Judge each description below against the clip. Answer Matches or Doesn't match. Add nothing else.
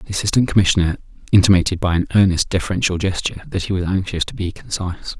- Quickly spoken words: Doesn't match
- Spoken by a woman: Doesn't match